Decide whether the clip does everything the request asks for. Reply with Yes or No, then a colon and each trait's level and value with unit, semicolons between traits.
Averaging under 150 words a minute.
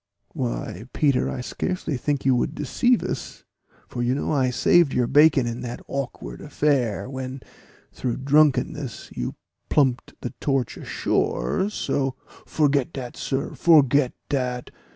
Yes: average, 140 wpm